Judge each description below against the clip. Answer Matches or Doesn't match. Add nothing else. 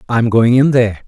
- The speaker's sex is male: Matches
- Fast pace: Matches